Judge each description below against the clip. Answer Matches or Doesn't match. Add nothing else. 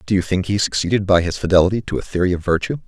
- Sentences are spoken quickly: Matches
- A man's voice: Matches